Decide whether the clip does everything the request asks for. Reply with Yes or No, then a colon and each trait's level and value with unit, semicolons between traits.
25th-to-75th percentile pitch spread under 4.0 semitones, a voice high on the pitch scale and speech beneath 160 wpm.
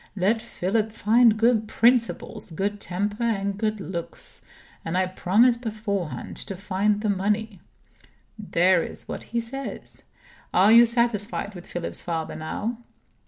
Yes: average, 3.4 semitones; high, 210 Hz; slow, 135 wpm